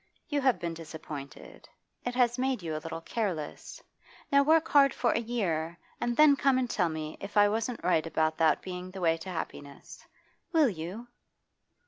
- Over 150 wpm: Yes, average, 180 wpm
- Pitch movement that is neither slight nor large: No, wide, 7.2 semitones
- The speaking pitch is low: No, high, 190 Hz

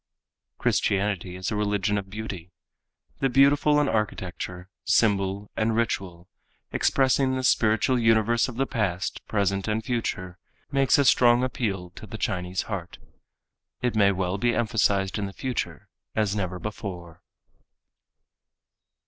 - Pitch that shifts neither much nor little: Yes, average, 3.8 semitones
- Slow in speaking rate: Yes, slow, 130 wpm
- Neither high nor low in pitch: No, low, 105 Hz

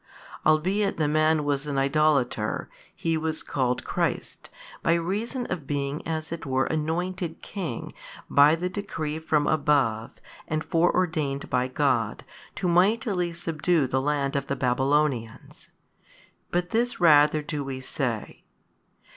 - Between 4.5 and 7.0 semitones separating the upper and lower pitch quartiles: No, average, 3.7 semitones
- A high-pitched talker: No, medium, 155 Hz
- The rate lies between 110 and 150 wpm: Yes, average, 140 wpm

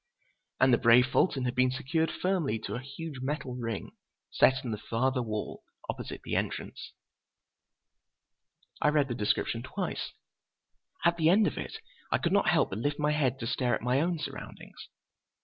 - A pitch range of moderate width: Yes, average, 4.5 semitones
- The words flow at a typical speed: Yes, average, 175 wpm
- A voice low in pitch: Yes, low, 130 Hz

